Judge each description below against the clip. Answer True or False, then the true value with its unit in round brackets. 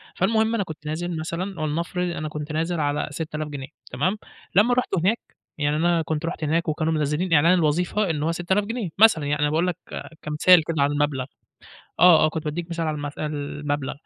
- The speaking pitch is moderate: True (160 Hz)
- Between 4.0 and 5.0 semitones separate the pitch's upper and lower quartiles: False (3.0 semitones)